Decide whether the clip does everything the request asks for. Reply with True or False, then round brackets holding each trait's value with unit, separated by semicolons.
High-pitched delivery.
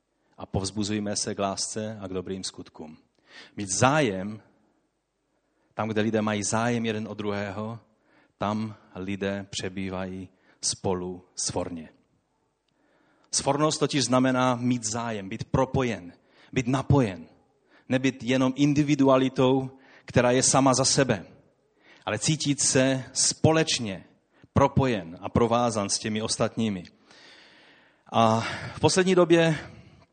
False (115 Hz)